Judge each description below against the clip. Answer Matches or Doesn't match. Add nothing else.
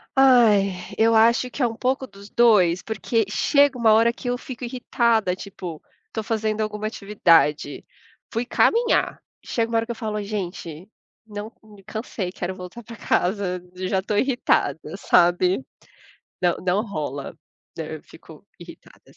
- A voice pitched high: Matches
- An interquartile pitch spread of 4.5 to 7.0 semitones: Doesn't match